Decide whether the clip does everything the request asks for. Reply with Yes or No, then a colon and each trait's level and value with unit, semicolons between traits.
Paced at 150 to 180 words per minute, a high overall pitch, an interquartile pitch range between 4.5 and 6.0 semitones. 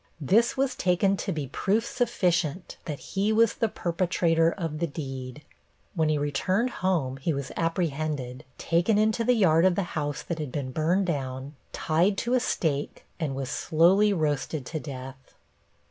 No: average, 165 wpm; medium, 165 Hz; average, 4.9 semitones